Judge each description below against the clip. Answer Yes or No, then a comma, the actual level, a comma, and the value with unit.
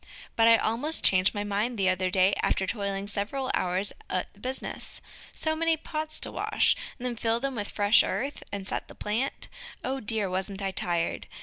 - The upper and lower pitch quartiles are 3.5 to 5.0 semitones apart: Yes, average, 4.7 semitones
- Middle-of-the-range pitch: No, high, 210 Hz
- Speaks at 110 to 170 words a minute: No, average, 185 wpm